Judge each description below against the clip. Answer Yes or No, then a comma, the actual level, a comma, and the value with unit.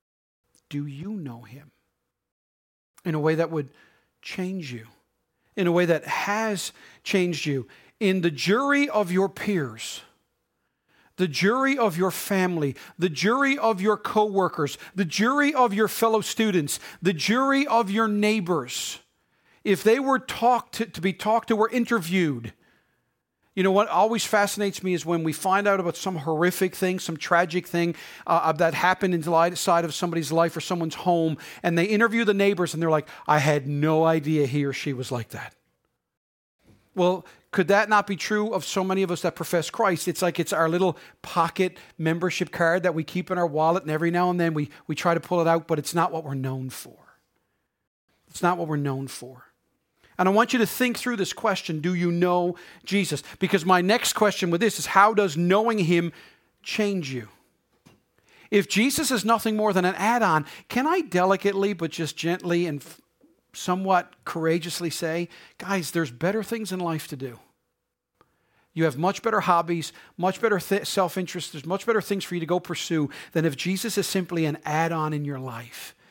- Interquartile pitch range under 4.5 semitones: Yes, average, 3.8 semitones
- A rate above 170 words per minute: Yes, average, 190 wpm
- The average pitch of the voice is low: No, medium, 180 Hz